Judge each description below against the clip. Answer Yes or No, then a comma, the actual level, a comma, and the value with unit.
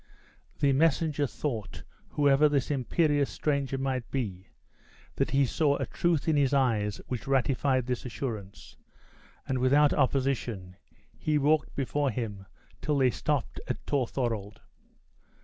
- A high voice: No, low, 135 Hz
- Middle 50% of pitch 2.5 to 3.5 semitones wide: Yes, average, 3.2 semitones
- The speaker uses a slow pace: Yes, slow, 130 wpm